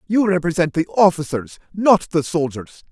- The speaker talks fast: No, average, 145 wpm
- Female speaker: No, male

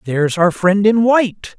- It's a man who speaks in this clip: Yes, male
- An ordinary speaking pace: Yes, average, 190 wpm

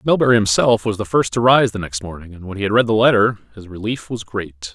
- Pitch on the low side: Yes, low, 105 Hz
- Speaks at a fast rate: Yes, fast, 265 wpm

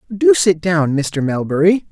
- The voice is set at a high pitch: No, medium, 165 Hz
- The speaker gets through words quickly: No, average, 155 wpm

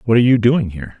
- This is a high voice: No, low, 115 Hz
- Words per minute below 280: No, fast, 300 wpm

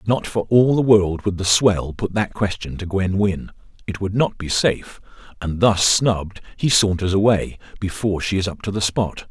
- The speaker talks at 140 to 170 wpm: No, fast, 205 wpm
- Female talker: No, male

